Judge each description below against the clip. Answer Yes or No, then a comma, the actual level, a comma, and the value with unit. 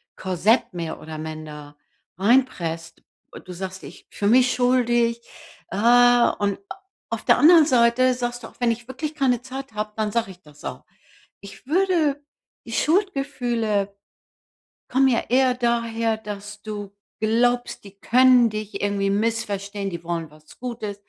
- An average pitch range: Yes, average, 4.0 semitones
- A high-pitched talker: Yes, high, 225 Hz